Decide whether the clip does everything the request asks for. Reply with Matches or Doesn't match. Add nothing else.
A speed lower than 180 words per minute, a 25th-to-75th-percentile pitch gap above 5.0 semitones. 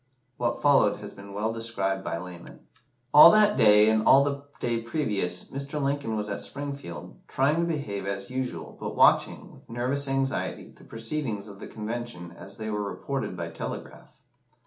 Matches